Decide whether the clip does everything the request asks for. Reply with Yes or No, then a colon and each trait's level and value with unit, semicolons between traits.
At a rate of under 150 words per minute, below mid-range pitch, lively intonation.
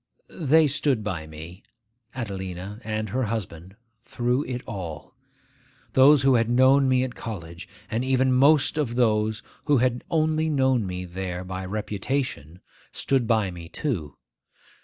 Yes: average, 140 wpm; low, 115 Hz; wide, 5.9 semitones